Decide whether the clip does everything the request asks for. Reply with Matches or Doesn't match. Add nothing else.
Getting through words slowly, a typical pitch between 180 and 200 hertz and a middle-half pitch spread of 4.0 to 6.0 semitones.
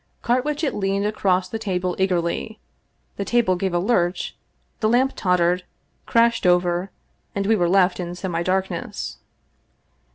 Doesn't match